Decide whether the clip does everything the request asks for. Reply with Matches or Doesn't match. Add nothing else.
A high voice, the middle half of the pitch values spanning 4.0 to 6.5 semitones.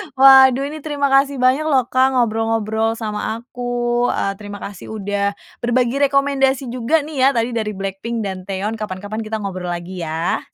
Matches